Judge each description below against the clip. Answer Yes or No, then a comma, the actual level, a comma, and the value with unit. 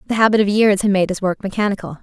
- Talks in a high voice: Yes, high, 200 Hz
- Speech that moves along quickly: Yes, fast, 265 wpm